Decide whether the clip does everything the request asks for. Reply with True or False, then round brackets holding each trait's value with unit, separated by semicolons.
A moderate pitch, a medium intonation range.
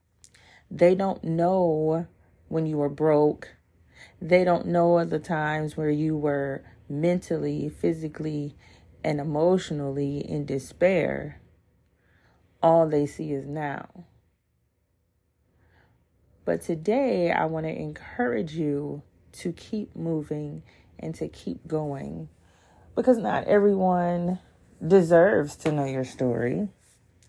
False (150 Hz; 7.5 semitones)